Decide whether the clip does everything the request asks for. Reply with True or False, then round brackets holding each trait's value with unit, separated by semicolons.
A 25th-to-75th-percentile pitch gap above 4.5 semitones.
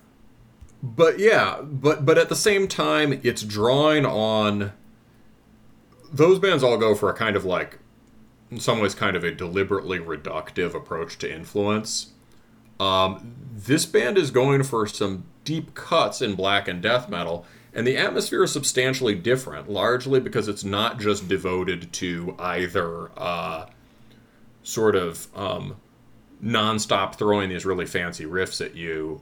True (4.9 semitones)